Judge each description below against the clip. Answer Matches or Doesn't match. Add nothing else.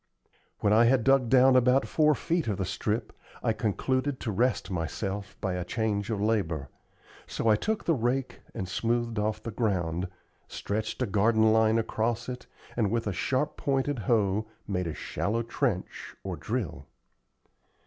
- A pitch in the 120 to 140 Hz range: Doesn't match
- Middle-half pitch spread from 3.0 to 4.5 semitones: Matches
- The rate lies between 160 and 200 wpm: Matches